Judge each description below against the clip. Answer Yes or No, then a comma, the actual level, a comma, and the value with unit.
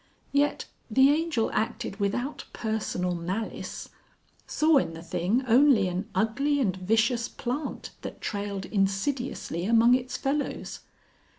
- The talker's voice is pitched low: No, high, 225 Hz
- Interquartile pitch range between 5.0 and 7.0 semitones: Yes, wide, 5.6 semitones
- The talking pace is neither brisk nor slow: No, slow, 120 wpm